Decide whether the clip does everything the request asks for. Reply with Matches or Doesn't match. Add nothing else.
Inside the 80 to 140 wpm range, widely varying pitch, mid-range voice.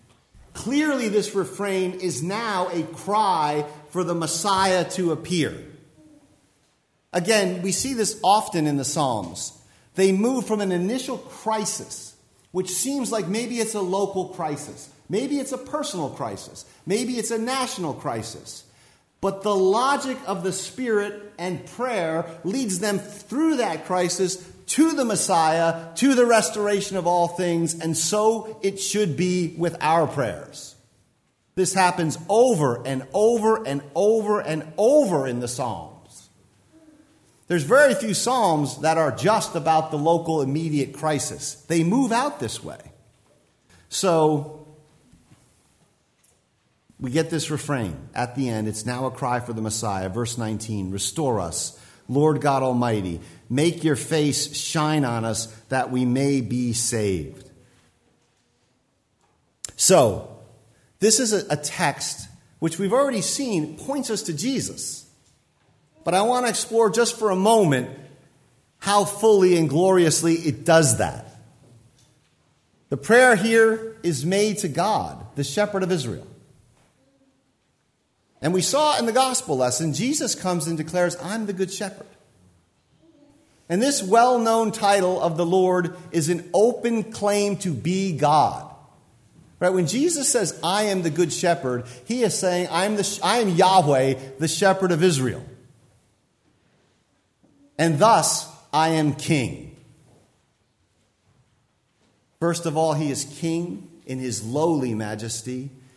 Matches